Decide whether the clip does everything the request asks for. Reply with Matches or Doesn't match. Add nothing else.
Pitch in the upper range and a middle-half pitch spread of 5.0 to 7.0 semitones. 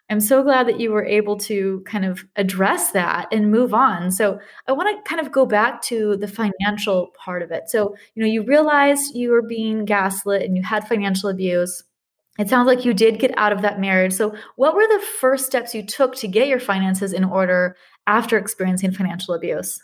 Doesn't match